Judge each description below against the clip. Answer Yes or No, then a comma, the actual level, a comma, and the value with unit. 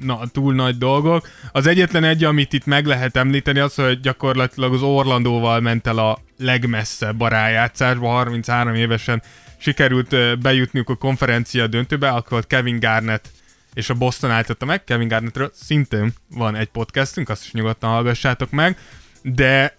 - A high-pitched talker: No, low, 125 Hz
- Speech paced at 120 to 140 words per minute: No, fast, 155 wpm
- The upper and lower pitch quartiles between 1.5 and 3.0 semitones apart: Yes, average, 2.7 semitones